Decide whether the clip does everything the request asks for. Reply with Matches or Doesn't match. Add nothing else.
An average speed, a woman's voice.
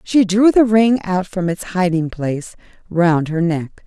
Matches